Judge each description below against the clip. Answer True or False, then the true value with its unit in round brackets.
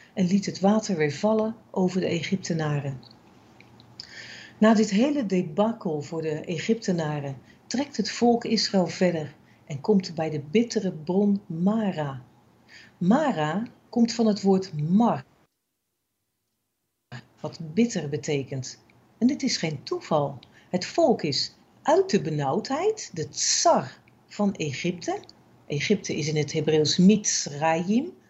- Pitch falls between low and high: True (180 Hz)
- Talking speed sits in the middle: False (125 wpm)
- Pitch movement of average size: False (6.1 semitones)